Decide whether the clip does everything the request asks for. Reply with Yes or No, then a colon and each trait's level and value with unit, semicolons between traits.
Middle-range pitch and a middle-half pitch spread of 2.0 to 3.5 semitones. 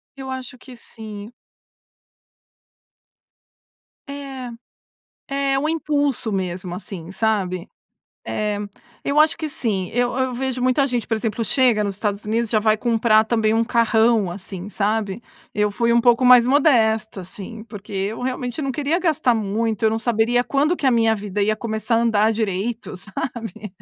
No: high, 225 Hz; average, 3.2 semitones